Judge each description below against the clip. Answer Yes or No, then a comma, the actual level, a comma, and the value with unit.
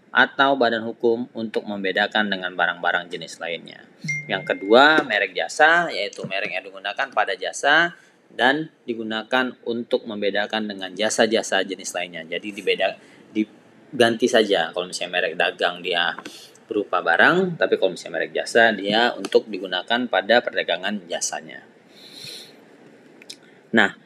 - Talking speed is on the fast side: No, average, 125 wpm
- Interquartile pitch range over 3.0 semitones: Yes, average, 3.6 semitones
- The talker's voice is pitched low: Yes, low, 110 Hz